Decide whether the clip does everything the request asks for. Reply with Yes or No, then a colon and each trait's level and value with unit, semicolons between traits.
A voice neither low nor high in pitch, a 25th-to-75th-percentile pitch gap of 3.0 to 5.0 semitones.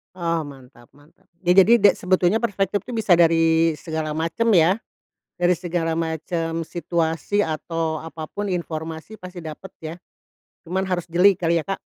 No: medium, 170 Hz; narrow, 2.5 semitones